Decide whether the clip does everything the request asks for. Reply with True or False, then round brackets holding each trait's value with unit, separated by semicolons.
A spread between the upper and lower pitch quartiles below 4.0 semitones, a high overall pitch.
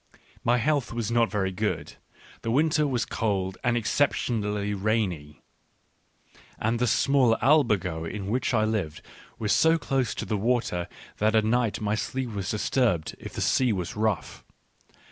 False (3.4 semitones; 110 Hz)